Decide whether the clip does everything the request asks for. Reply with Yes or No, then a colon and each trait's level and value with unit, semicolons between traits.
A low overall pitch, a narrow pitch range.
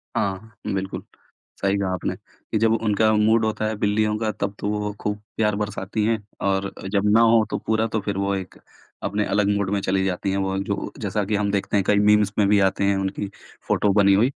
Yes: low, 105 Hz; narrow, 1.4 semitones